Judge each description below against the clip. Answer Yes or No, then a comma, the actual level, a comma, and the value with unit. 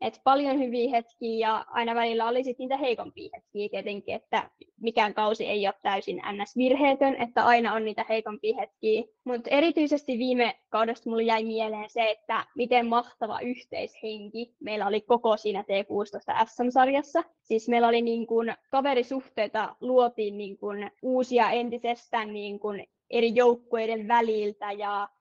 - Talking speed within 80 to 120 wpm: No, average, 150 wpm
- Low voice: No, high, 230 Hz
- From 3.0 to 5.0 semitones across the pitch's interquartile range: No, narrow, 2.5 semitones